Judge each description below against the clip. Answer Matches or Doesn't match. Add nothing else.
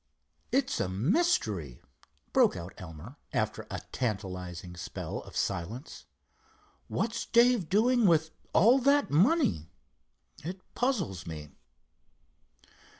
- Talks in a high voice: Doesn't match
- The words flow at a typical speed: Doesn't match